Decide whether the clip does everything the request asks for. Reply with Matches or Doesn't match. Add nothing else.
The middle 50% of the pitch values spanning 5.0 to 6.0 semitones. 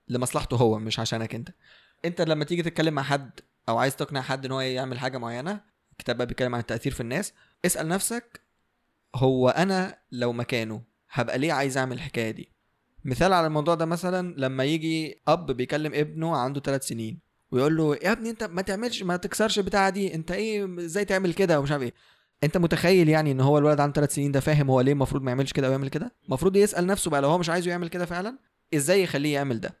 Matches